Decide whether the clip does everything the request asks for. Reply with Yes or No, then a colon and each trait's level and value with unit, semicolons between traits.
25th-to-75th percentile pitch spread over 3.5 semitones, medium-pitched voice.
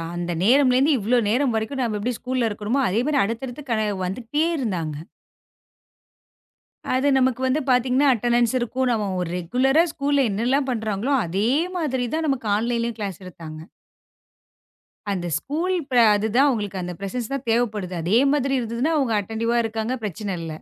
No: average, 4.0 semitones; high, 235 Hz